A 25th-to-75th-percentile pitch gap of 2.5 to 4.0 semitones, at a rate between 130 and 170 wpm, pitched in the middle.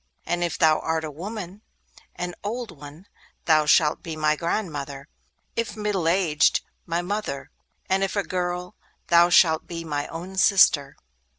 Yes: average, 3.5 semitones; average, 160 wpm; medium, 170 Hz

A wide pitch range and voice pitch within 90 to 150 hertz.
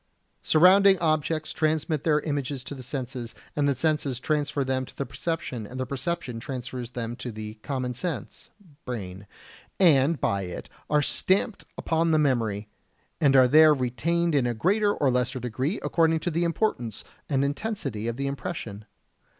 No: average, 4.4 semitones; medium, 140 Hz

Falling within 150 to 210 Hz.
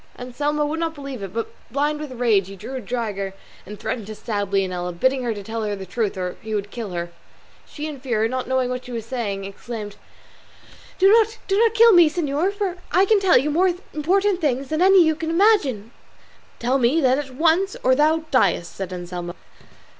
No: very high, 255 Hz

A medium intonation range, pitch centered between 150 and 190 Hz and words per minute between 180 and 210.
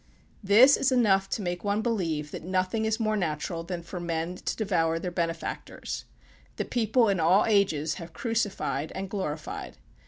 No: average, 4.5 semitones; medium, 185 Hz; average, 165 wpm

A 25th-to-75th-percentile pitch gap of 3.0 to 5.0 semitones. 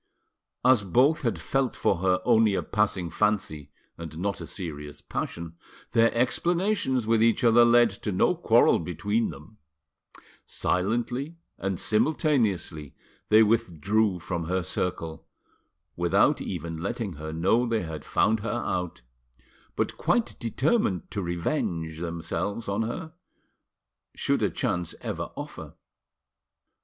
No: wide, 5.5 semitones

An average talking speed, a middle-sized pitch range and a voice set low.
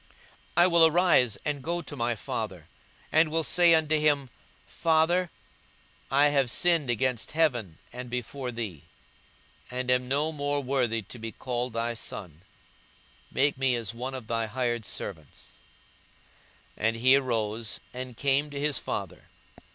Yes: average, 155 wpm; average, 4.2 semitones; low, 130 Hz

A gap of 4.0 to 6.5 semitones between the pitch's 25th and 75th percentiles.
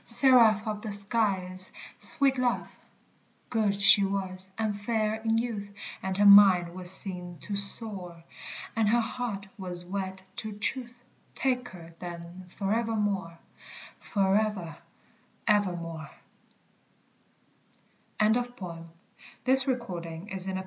No: average, 3.3 semitones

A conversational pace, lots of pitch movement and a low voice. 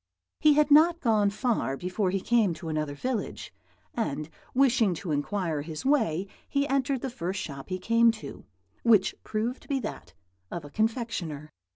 No: average, 170 wpm; wide, 7.2 semitones; high, 210 Hz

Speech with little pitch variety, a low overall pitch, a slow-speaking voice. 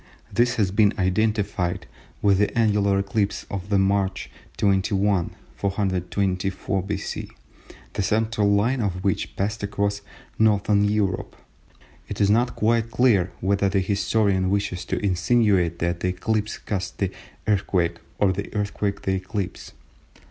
Yes: narrow, 1.8 semitones; low, 100 Hz; slow, 130 wpm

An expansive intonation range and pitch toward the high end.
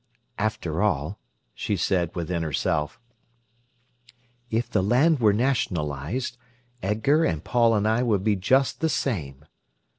No: wide, 6.4 semitones; low, 105 Hz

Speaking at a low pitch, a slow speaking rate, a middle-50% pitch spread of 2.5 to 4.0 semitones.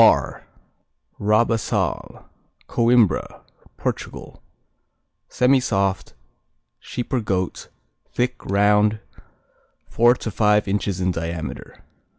Yes: low, 105 Hz; slow, 80 wpm; average, 3.5 semitones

